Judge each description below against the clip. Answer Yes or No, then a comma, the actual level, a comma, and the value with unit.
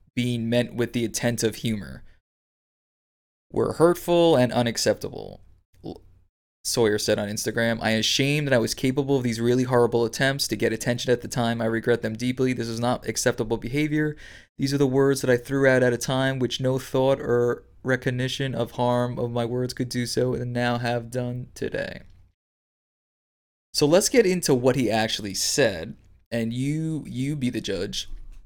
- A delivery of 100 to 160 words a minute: No, average, 175 wpm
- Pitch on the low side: Yes, low, 120 Hz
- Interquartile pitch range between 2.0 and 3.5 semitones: Yes, average, 2.8 semitones